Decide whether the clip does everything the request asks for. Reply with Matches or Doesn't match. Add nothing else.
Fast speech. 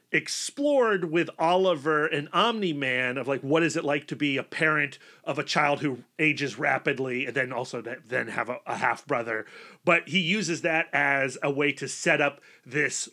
Doesn't match